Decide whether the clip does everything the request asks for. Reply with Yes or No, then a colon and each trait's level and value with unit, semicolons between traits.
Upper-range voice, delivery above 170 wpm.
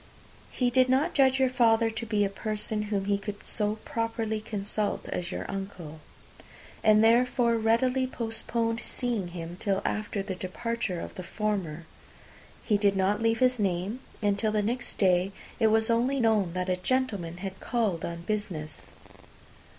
No: high, 215 Hz; average, 165 wpm